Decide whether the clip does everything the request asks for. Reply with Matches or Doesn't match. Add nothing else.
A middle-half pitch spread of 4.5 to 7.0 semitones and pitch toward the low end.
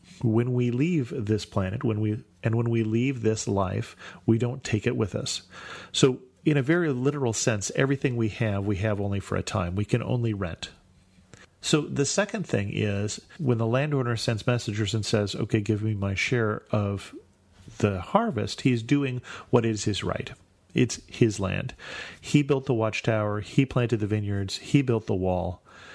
Doesn't match